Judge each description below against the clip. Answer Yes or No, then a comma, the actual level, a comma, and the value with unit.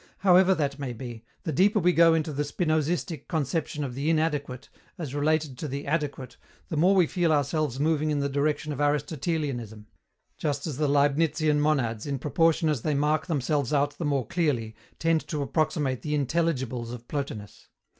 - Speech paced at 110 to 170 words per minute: No, average, 180 wpm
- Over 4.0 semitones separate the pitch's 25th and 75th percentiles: No, narrow, 2.5 semitones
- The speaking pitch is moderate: Yes, medium, 150 Hz